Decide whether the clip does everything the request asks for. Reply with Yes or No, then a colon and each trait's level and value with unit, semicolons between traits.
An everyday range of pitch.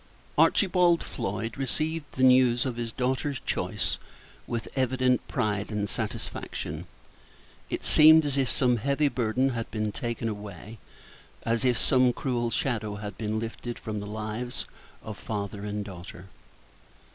Yes: average, 3.6 semitones